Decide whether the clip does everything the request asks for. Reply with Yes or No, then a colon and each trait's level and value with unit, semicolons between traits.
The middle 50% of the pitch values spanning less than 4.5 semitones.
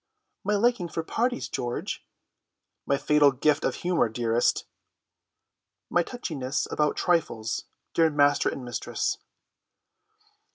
No: average, 5.3 semitones